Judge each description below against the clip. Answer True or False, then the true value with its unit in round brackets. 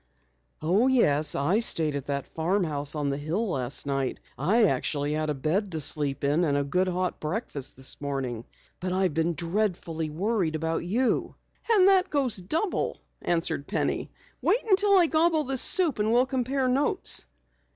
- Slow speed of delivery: False (170 wpm)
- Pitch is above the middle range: False (175 Hz)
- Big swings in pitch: True (8.6 semitones)